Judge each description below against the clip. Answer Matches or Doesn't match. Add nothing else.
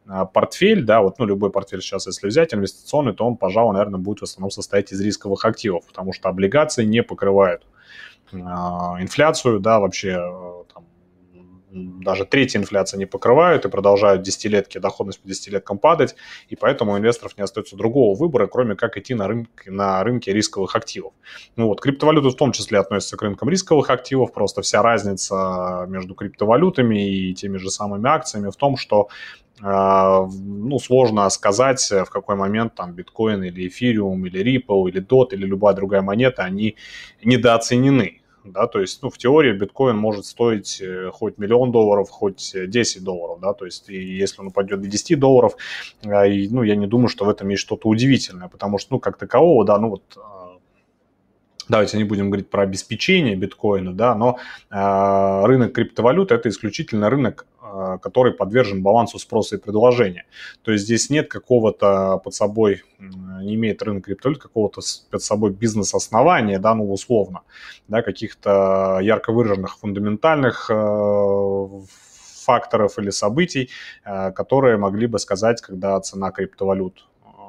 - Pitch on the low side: Matches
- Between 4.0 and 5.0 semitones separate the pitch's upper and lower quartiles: Doesn't match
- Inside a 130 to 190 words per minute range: Matches